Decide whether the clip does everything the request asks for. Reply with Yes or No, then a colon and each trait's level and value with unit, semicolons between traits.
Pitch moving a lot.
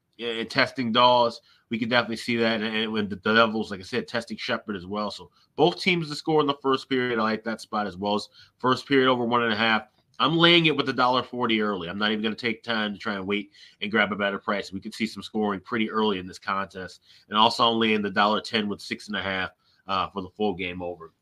No: average, 2.8 semitones